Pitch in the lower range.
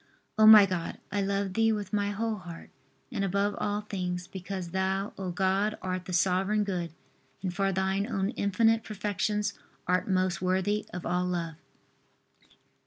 No: high, 195 Hz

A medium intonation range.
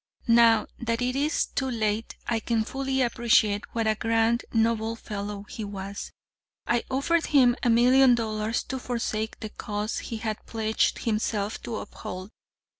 No: narrow, 2.0 semitones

